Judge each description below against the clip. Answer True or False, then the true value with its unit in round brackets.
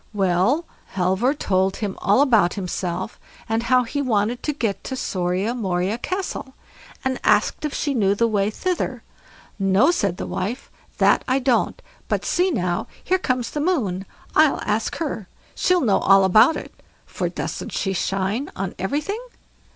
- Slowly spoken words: False (165 wpm)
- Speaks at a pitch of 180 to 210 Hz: False (220 Hz)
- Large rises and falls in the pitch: True (6.1 semitones)